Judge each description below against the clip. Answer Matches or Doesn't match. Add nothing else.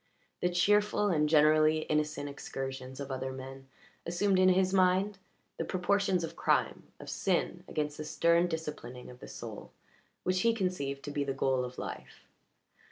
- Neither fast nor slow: Matches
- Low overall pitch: Doesn't match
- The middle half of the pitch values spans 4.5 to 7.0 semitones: Matches